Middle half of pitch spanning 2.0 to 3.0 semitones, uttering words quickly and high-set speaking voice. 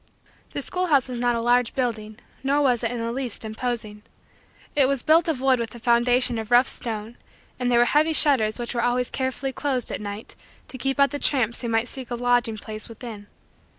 Yes: narrow, 2.4 semitones; fast, 215 wpm; high, 245 Hz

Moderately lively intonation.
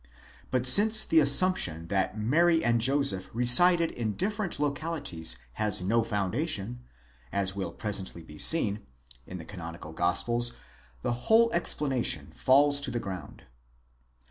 No: wide, 7.6 semitones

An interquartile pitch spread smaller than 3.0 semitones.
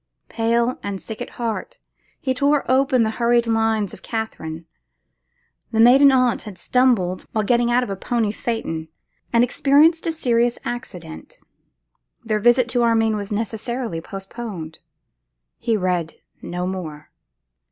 No: average, 3.8 semitones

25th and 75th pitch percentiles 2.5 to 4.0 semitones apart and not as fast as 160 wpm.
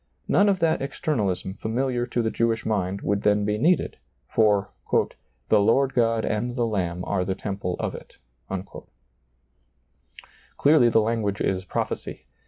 Yes: average, 3.3 semitones; average, 150 wpm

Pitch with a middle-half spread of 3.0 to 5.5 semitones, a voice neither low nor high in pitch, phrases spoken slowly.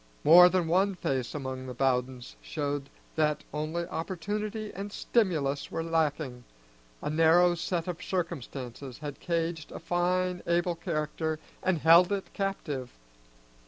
Yes: average, 3.8 semitones; medium, 165 Hz; slow, 130 wpm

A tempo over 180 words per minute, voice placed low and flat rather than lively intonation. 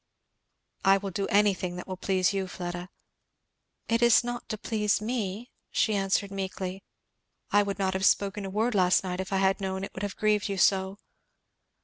No: average, 195 wpm; high, 195 Hz; narrow, 1.6 semitones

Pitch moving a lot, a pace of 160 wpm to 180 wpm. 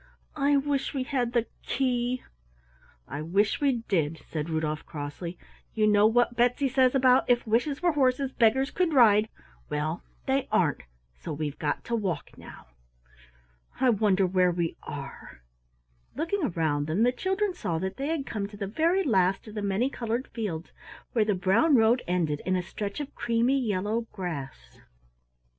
Yes: wide, 6.4 semitones; average, 165 wpm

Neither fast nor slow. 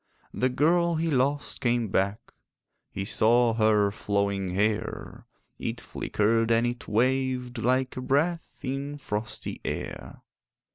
No: slow, 125 wpm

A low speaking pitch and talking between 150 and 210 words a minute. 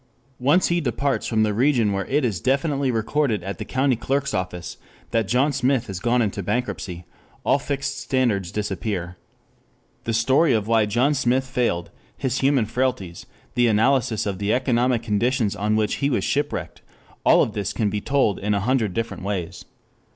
Yes: low, 115 Hz; average, 175 wpm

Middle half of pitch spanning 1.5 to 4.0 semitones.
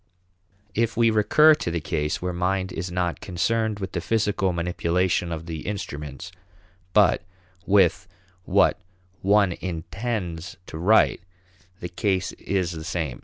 Yes: average, 3.2 semitones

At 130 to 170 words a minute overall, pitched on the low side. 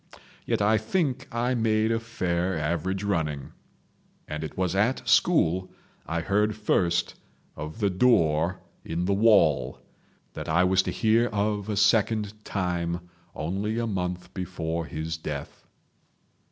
Yes: slow, 135 wpm; very low, 95 Hz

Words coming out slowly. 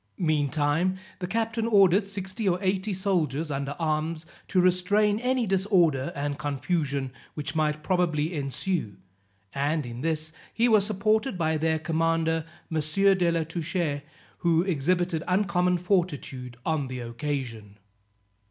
Yes: slow, 130 wpm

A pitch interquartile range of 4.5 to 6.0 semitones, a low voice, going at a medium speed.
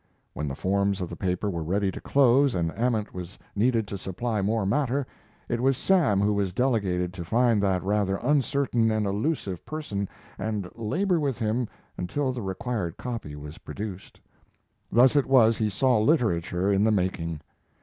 Yes: average, 4.8 semitones; low, 105 Hz; average, 170 wpm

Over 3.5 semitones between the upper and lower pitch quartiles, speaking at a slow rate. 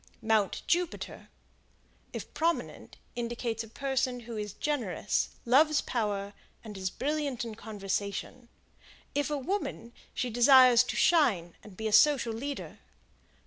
Yes: average, 4.6 semitones; slow, 130 wpm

